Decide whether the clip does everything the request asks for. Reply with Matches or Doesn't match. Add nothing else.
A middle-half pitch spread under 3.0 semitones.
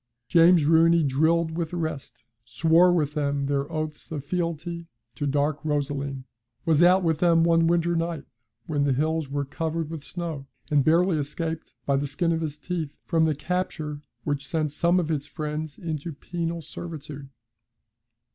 Matches